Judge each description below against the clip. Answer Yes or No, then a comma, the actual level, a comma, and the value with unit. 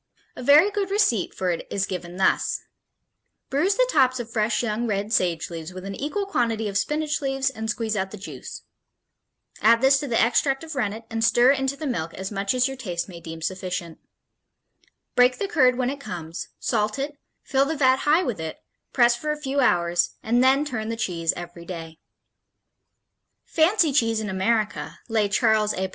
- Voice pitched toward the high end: Yes, high, 230 Hz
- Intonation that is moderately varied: No, wide, 6.1 semitones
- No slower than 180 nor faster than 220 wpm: Yes, average, 190 wpm